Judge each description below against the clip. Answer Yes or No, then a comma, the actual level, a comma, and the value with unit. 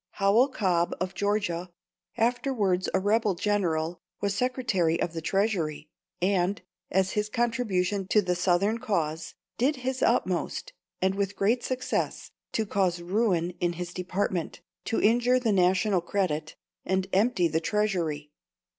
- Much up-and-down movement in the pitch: No, average, 3.6 semitones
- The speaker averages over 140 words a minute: No, slow, 135 wpm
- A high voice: Yes, high, 195 Hz